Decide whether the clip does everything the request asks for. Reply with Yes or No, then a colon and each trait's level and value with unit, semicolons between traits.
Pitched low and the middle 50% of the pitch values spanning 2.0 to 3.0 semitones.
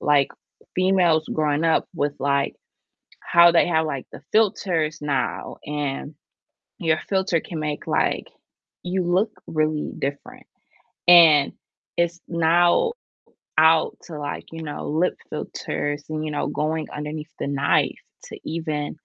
No: medium, 155 Hz; narrow, 2.6 semitones